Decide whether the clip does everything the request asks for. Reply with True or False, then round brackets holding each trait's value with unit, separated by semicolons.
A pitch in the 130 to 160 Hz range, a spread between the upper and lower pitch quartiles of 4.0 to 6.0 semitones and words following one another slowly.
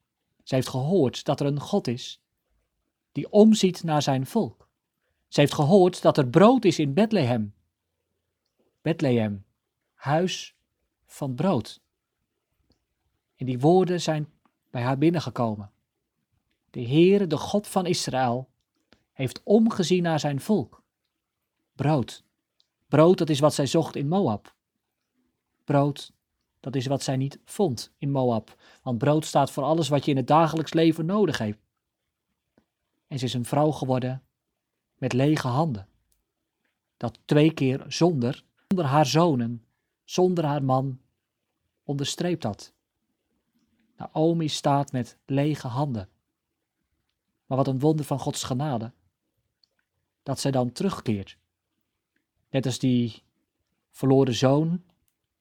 True (140 Hz; 4.4 semitones; 125 wpm)